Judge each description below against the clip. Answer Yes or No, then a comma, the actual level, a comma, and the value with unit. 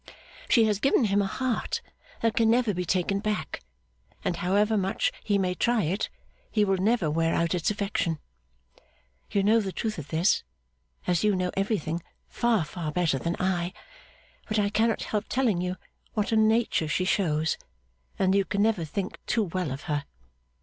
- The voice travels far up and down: No, average, 3.7 semitones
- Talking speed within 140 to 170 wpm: No, average, 180 wpm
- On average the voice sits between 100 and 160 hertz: No, high, 195 Hz